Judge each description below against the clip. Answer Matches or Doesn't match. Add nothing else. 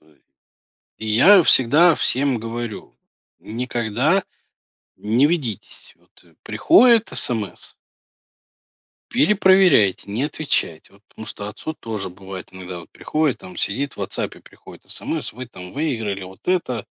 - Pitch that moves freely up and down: Matches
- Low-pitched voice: Matches